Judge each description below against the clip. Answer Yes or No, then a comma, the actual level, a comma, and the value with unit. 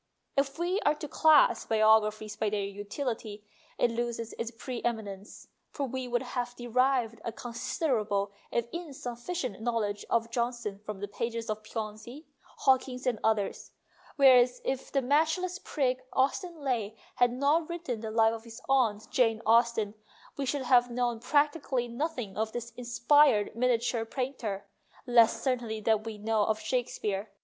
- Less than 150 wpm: No, average, 155 wpm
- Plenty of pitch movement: No, average, 3.2 semitones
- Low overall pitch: No, high, 235 Hz